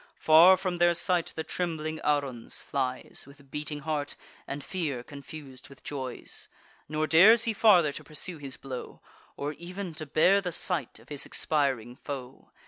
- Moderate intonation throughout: Yes, average, 3.9 semitones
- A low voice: No, medium, 150 Hz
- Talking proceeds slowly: No, average, 160 wpm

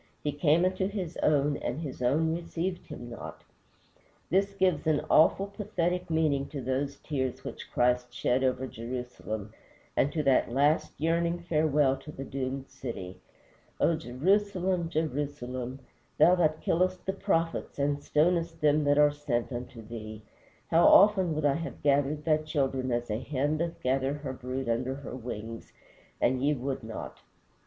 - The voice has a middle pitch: Yes, medium, 145 Hz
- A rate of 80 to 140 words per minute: No, average, 160 wpm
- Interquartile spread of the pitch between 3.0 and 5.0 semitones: Yes, average, 4.3 semitones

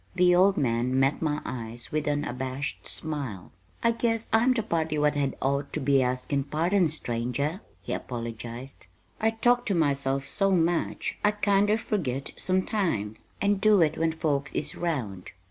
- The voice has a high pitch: No, medium, 150 Hz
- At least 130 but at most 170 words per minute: Yes, average, 165 wpm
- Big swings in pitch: Yes, wide, 6.4 semitones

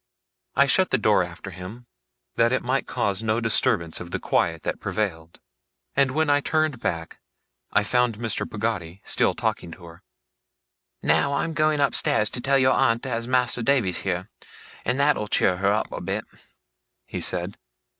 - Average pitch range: No, wide, 6.2 semitones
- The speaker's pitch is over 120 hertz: No, low, 115 Hz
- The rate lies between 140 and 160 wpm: No, average, 175 wpm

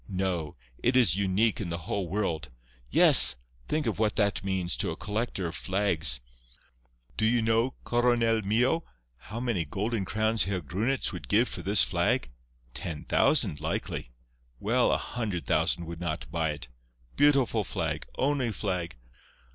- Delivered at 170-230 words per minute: No, average, 155 wpm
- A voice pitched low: Yes, low, 100 Hz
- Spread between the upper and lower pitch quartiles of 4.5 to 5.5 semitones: Yes, average, 5.0 semitones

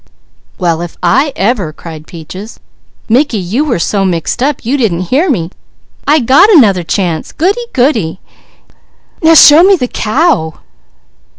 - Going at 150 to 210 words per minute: No, average, 140 wpm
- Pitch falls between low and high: No, high, 225 Hz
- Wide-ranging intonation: Yes, wide, 9.0 semitones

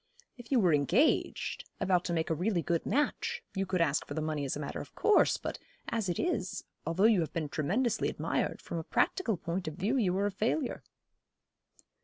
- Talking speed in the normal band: No, fast, 210 wpm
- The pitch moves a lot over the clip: Yes, wide, 5.9 semitones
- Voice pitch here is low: No, medium, 185 Hz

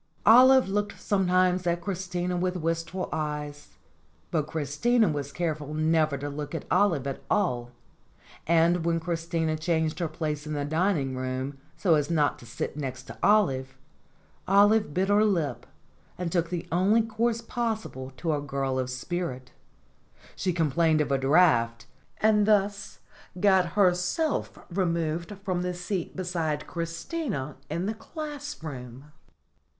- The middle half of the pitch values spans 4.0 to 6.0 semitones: Yes, average, 4.5 semitones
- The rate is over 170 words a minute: No, average, 140 wpm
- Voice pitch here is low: No, medium, 170 Hz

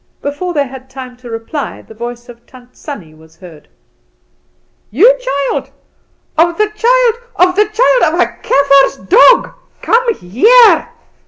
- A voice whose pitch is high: Yes, very high, 285 Hz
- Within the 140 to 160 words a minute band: Yes, average, 145 wpm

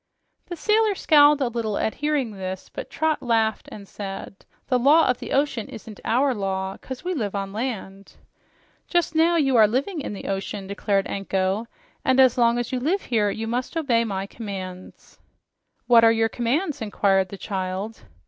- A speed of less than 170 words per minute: No, average, 180 wpm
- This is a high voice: Yes, high, 230 Hz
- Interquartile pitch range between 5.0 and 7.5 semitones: Yes, wide, 5.6 semitones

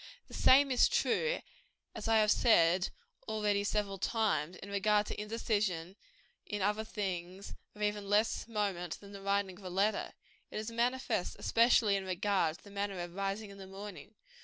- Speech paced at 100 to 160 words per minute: No, average, 175 wpm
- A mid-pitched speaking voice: No, high, 205 Hz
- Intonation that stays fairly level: Yes, narrow, 2.0 semitones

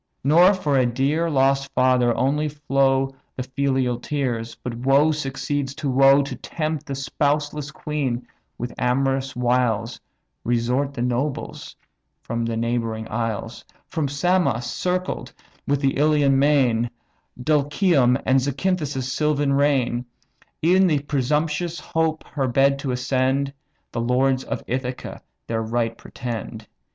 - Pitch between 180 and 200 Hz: No, low, 135 Hz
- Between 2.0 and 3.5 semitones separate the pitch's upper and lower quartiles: Yes, average, 3.0 semitones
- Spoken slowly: Yes, slow, 130 wpm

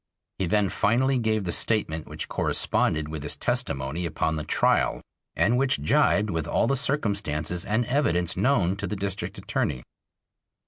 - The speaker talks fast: No, average, 155 wpm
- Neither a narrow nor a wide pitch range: No, wide, 6.8 semitones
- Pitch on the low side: Yes, low, 100 Hz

